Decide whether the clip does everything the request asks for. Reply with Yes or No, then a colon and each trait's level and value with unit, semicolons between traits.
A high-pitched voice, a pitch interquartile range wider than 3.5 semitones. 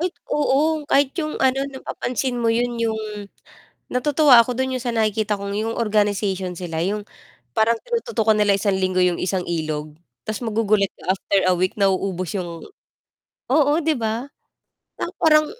Yes: high, 220 Hz; average, 4.9 semitones